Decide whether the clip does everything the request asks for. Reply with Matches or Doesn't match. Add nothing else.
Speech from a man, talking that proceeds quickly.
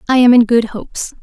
Doesn't match